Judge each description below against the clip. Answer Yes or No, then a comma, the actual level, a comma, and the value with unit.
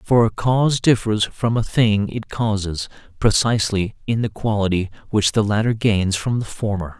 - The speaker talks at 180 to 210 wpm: No, average, 170 wpm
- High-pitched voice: No, low, 105 Hz